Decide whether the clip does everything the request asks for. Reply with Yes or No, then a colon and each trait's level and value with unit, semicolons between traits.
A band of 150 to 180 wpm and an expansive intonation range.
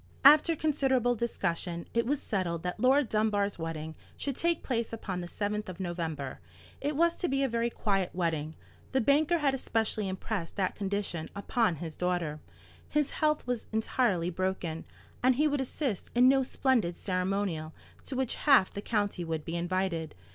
Yes: average, 170 wpm; wide, 6.9 semitones